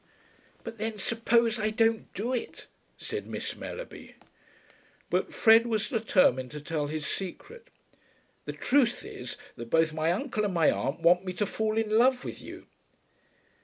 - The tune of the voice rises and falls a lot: Yes, wide, 5.7 semitones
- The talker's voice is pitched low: No, high, 215 Hz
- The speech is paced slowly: No, average, 160 wpm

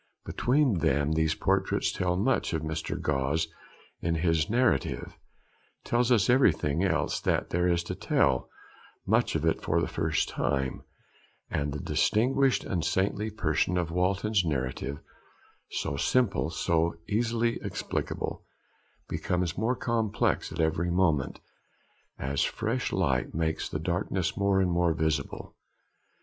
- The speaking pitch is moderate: No, very low, 85 Hz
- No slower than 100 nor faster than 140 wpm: Yes, slow, 135 wpm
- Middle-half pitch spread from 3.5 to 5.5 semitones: Yes, average, 4.7 semitones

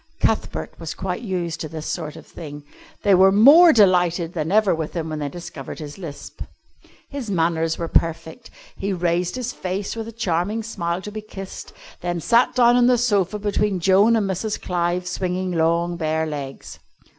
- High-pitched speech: No, medium, 180 Hz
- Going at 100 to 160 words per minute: No, average, 180 wpm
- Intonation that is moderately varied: Yes, average, 4.2 semitones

